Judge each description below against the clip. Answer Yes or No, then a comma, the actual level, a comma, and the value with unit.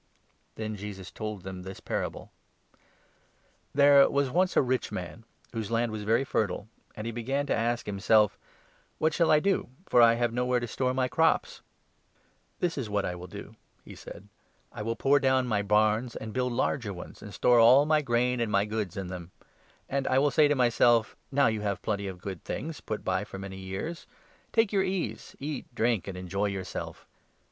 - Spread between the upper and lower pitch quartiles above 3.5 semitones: Yes, average, 4.7 semitones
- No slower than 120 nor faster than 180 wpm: No, fast, 205 wpm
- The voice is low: Yes, low, 115 Hz